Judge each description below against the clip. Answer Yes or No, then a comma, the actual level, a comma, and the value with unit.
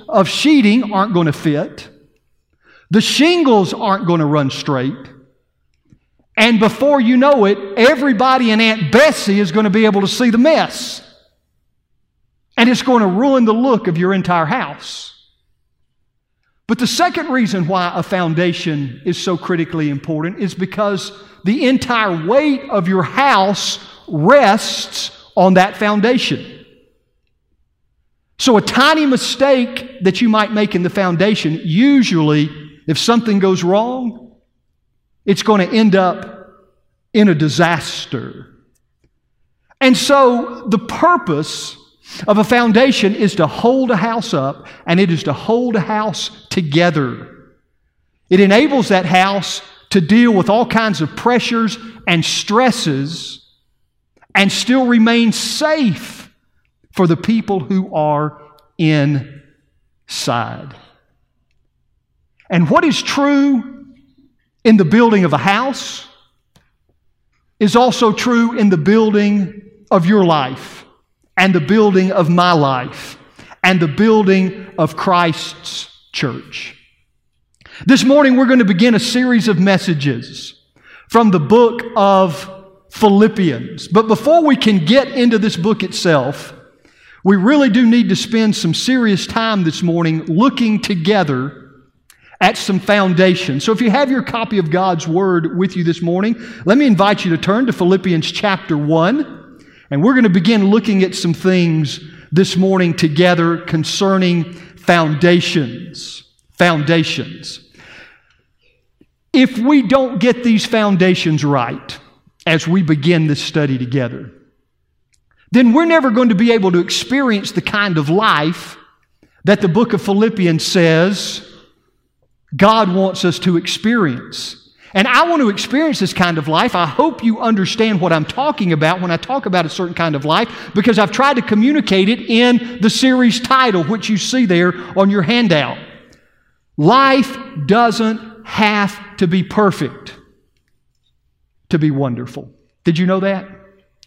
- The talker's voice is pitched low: No, high, 195 Hz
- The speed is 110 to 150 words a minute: Yes, average, 140 wpm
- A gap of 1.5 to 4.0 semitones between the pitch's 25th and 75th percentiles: No, average, 5.1 semitones